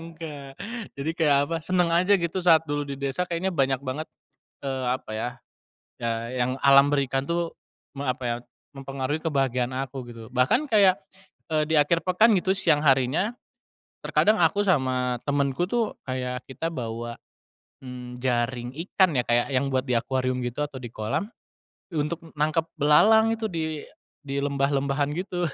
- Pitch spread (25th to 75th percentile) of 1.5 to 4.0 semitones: No, average, 4.5 semitones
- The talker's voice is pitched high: No, medium, 140 Hz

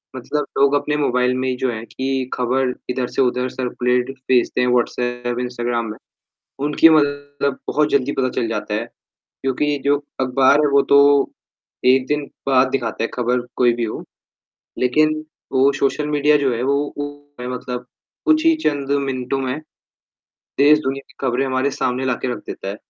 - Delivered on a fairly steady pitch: Yes, narrow, 2.3 semitones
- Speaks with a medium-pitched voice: No, low, 130 Hz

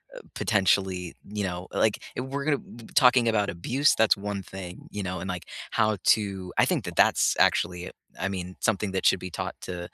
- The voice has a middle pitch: No, very low, 95 Hz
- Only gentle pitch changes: No, average, 3.2 semitones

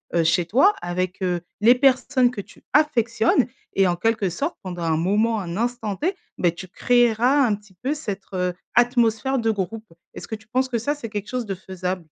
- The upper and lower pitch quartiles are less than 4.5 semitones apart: No, average, 4.9 semitones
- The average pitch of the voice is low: No, high, 220 Hz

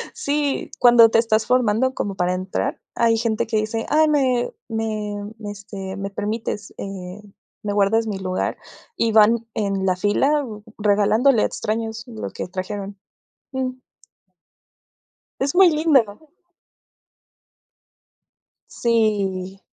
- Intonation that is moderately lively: Yes, average, 3.2 semitones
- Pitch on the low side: No, high, 220 Hz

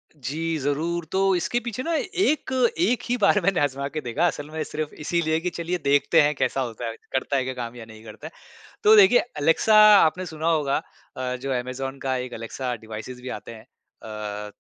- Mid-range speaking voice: Yes, medium, 145 Hz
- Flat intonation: No, average, 5.3 semitones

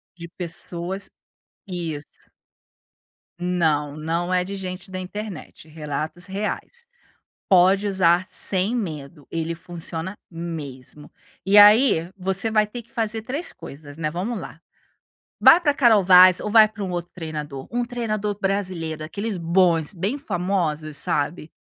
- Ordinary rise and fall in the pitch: Yes, average, 4.1 semitones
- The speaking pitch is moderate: Yes, medium, 180 Hz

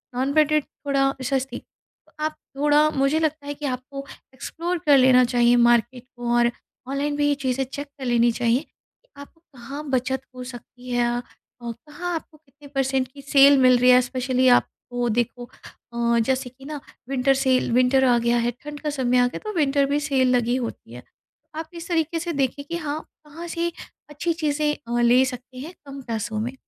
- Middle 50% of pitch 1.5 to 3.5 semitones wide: Yes, average, 3.0 semitones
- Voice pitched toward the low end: No, very high, 265 Hz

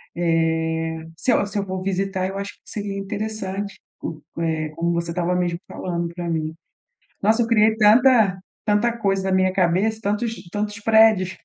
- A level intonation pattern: No, average, 3.6 semitones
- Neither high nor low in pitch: No, high, 195 Hz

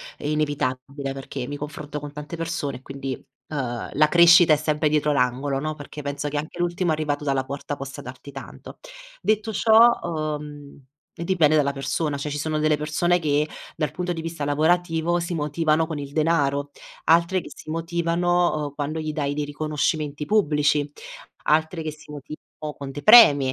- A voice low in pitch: No, medium, 150 Hz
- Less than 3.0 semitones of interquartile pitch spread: Yes, narrow, 2.4 semitones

